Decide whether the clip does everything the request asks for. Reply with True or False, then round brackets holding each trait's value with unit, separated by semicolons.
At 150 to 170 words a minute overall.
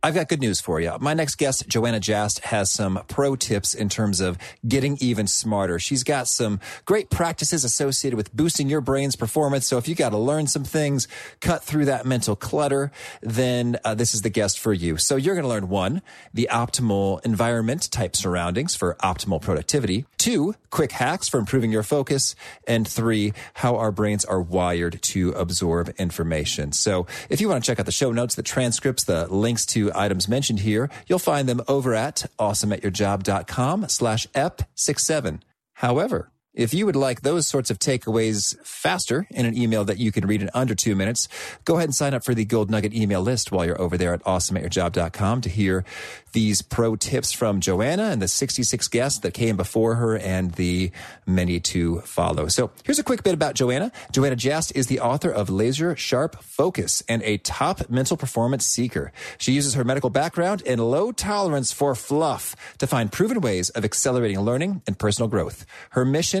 False (190 wpm)